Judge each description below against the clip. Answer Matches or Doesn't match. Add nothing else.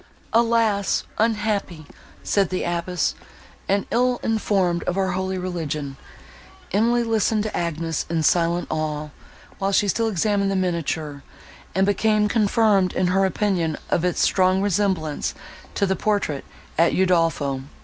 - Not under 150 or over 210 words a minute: Doesn't match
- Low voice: Doesn't match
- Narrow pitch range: Doesn't match